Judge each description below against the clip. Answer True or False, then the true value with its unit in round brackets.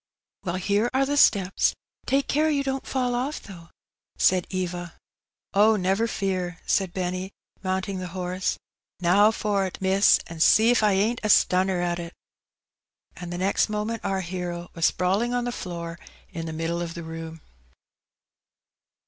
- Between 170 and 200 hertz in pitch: True (190 Hz)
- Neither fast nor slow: True (170 wpm)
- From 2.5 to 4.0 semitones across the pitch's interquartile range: True (3.4 semitones)